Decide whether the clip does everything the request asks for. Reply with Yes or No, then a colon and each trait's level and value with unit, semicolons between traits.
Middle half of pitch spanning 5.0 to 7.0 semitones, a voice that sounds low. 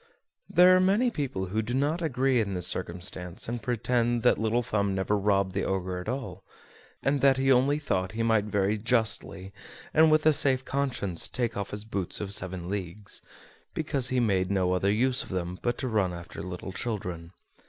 Yes: average, 5.3 semitones; low, 105 Hz